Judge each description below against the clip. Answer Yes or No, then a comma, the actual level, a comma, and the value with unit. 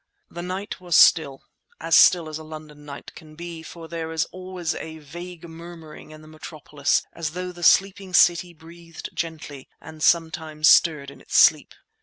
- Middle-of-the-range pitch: Yes, medium, 160 Hz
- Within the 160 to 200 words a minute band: Yes, average, 170 wpm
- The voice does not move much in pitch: Yes, narrow, 1.9 semitones